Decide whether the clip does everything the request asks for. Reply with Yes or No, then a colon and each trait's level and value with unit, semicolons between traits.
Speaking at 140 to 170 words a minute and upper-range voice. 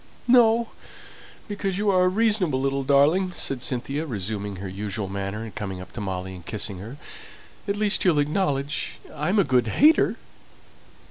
No: average, 160 wpm; medium, 140 Hz